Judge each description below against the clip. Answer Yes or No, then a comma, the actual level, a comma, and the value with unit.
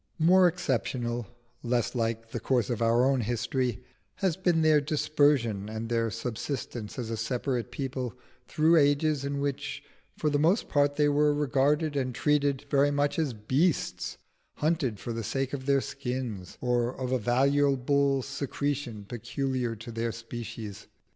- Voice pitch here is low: Yes, low, 130 Hz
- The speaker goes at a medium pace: Yes, average, 155 wpm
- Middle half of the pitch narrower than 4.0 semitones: Yes, average, 3.5 semitones